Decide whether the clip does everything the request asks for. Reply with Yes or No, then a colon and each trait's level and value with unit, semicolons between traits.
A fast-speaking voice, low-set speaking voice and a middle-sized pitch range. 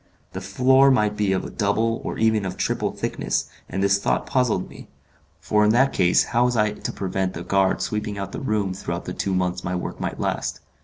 Yes: fast, 215 wpm; low, 100 Hz; average, 3.0 semitones